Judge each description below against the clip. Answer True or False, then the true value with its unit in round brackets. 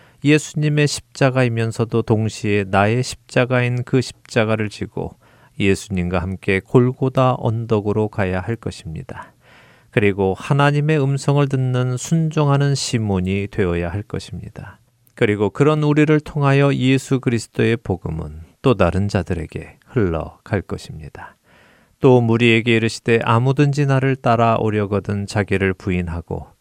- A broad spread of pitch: False (4.7 semitones)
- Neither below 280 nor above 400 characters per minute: True (310 characters per minute)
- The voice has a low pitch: True (115 Hz)